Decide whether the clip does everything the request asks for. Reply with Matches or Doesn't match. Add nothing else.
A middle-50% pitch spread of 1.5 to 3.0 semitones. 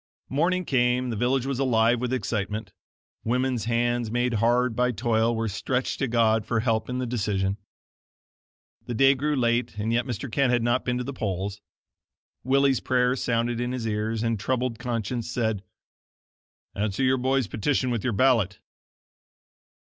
Matches